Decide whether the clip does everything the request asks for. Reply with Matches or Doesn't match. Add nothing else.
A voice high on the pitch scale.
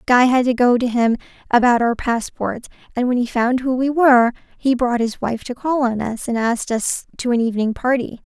Matches